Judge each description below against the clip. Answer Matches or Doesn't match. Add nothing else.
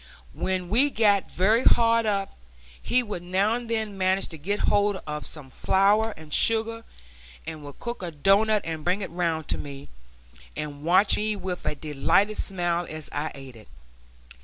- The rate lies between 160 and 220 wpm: Matches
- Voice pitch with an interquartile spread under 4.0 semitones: Doesn't match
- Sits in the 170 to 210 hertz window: Matches